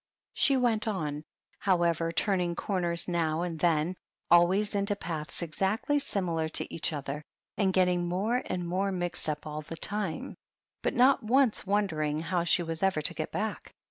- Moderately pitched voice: Yes, medium, 175 Hz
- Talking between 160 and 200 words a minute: Yes, average, 165 wpm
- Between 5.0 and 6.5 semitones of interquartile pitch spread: No, average, 3.6 semitones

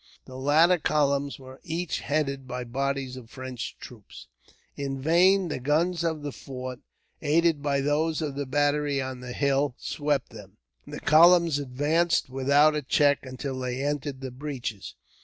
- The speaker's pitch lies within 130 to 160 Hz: Yes, medium, 140 Hz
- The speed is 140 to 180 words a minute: Yes, average, 160 wpm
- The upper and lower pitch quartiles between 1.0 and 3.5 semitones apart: Yes, narrow, 2.6 semitones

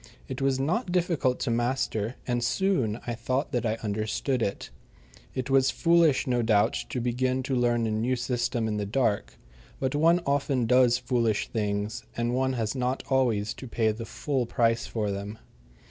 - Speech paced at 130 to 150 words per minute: No, average, 175 wpm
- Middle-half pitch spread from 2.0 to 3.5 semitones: Yes, average, 2.9 semitones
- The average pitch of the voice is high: No, low, 120 Hz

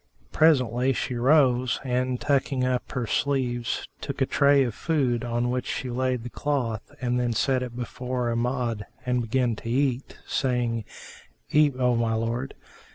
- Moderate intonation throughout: No, narrow, 1.7 semitones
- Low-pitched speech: Yes, low, 125 Hz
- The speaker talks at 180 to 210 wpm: No, average, 160 wpm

